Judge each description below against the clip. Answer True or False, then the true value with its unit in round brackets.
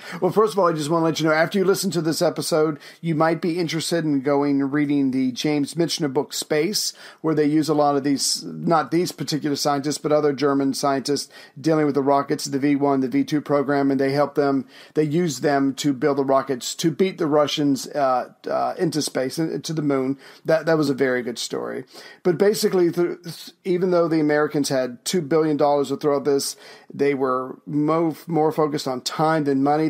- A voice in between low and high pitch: True (150 Hz)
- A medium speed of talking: False (215 wpm)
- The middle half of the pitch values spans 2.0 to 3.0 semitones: True (2.5 semitones)